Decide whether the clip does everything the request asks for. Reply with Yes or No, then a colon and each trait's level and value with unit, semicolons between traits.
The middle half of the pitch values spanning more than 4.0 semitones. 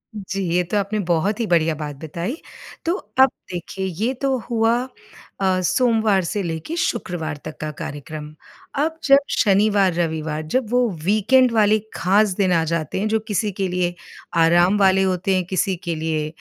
Yes: average, 4.5 semitones